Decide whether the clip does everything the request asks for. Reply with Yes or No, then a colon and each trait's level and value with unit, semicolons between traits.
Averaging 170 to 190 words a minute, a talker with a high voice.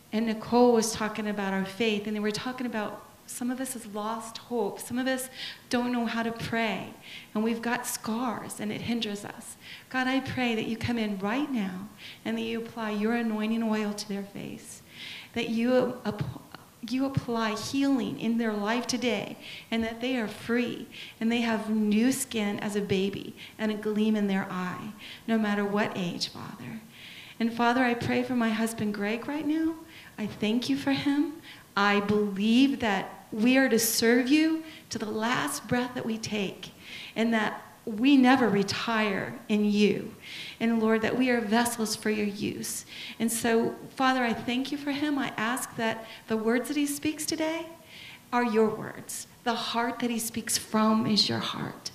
Yes: average, 185 wpm; high, 225 Hz